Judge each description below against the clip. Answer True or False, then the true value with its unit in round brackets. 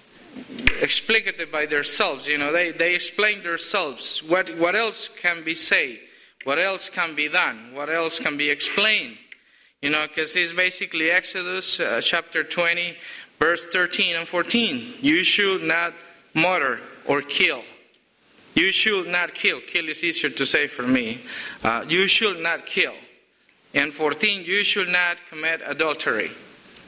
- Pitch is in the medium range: True (175 Hz)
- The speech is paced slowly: False (150 wpm)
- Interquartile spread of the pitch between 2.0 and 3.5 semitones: True (3.0 semitones)